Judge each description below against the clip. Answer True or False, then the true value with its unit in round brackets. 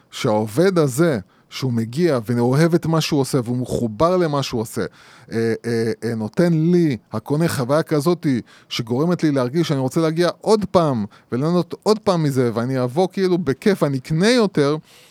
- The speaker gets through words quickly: True (165 wpm)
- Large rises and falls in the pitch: True (5.9 semitones)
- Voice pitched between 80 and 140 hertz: False (150 Hz)